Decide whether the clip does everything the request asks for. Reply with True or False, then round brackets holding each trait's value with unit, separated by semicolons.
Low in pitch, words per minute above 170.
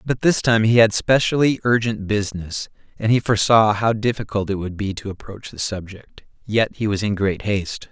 True (105 Hz; 195 wpm)